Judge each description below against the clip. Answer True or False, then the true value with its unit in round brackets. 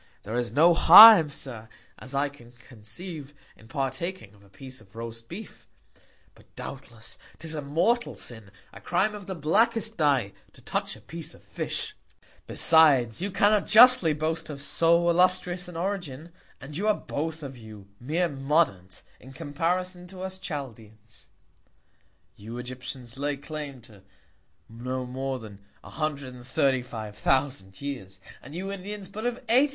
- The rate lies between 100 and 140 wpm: False (150 wpm)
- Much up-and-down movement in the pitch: True (6.5 semitones)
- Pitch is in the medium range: True (145 Hz)